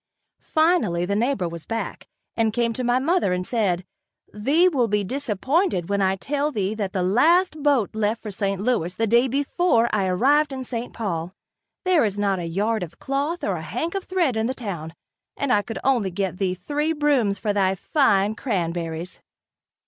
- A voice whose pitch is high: Yes, high, 220 Hz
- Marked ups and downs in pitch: Yes, wide, 6.4 semitones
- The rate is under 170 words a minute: No, average, 190 wpm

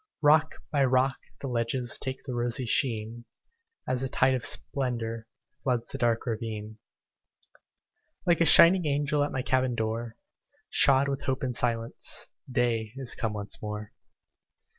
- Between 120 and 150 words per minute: Yes, average, 145 wpm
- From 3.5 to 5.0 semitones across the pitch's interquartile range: No, average, 3.0 semitones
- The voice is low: Yes, low, 125 Hz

